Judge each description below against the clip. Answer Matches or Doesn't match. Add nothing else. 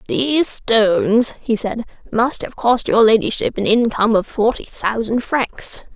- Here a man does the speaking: Doesn't match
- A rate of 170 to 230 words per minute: Doesn't match